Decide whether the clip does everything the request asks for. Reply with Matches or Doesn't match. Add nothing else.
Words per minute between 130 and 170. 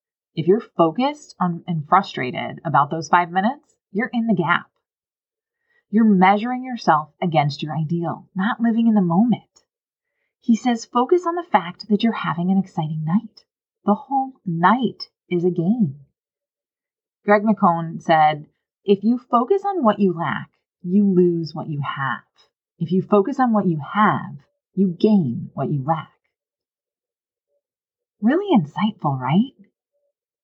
Matches